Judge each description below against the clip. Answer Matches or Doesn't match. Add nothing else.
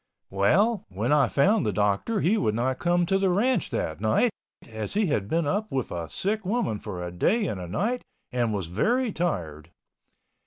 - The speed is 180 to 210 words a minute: Matches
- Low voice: Doesn't match